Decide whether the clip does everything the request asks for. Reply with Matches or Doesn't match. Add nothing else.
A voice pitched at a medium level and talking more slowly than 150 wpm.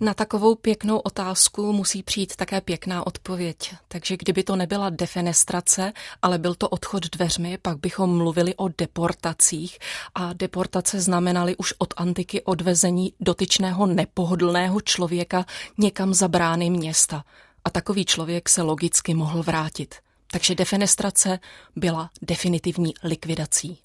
Matches